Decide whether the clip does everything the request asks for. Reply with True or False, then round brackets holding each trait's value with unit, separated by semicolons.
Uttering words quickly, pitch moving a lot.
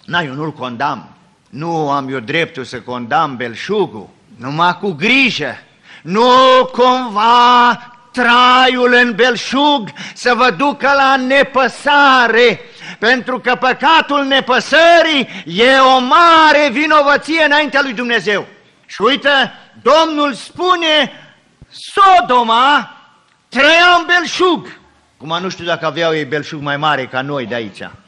False (120 wpm; 8.9 semitones)